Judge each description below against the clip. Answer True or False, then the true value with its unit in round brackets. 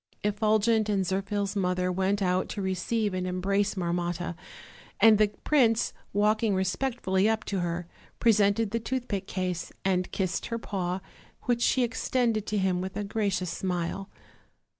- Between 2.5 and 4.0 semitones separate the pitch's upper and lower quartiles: True (2.9 semitones)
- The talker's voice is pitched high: True (200 Hz)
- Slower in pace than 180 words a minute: True (145 wpm)